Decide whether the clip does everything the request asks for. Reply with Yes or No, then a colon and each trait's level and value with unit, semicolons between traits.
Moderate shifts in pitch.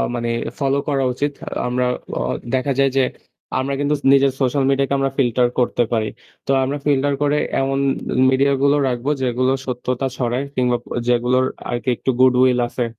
No: narrow, 1.9 semitones